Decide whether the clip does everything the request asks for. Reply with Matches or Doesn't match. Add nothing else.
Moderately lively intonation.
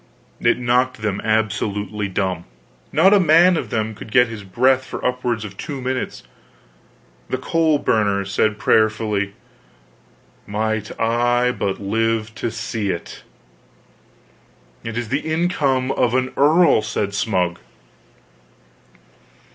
Matches